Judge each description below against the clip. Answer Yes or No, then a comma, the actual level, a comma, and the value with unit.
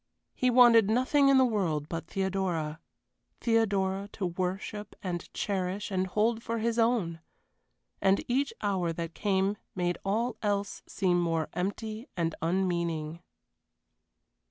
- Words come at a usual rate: No, slow, 130 wpm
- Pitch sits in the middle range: No, high, 195 Hz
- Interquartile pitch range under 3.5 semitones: No, average, 4.2 semitones